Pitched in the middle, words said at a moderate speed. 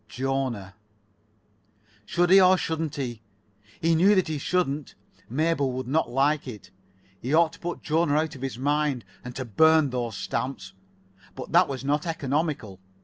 Yes: medium, 145 Hz; average, 160 wpm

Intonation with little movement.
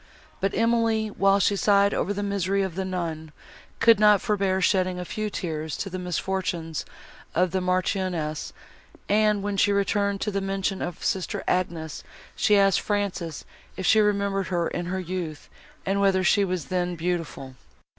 Yes: narrow, 2.2 semitones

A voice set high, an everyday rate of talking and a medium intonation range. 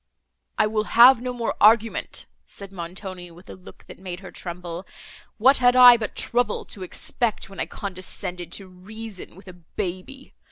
Yes: high, 195 Hz; average, 170 wpm; average, 4.2 semitones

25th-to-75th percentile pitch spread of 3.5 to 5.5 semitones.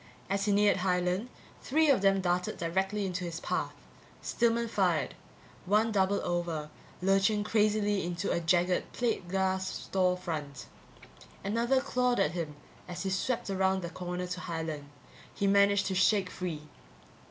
No: average, 2.7 semitones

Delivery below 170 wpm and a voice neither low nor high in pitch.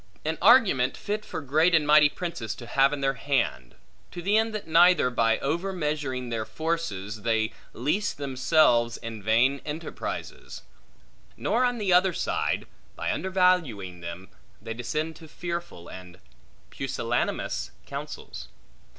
Yes: average, 140 wpm; medium, 145 Hz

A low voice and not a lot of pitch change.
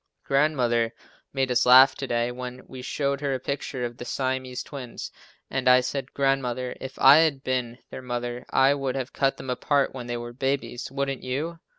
Yes: low, 130 Hz; narrow, 1.7 semitones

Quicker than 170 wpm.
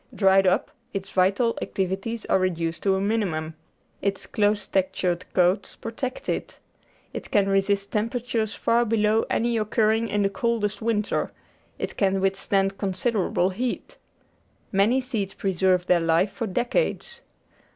No: average, 140 wpm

